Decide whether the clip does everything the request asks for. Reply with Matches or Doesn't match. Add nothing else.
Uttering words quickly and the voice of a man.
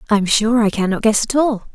Doesn't match